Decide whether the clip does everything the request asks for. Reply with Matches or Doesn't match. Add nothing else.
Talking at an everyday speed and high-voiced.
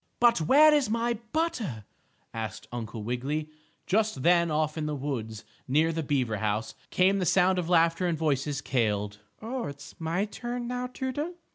Doesn't match